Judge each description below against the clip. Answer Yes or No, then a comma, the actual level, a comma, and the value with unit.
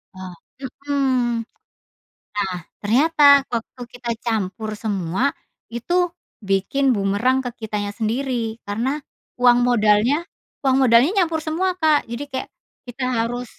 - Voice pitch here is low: No, high, 245 Hz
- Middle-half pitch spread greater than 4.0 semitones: Yes, average, 4.4 semitones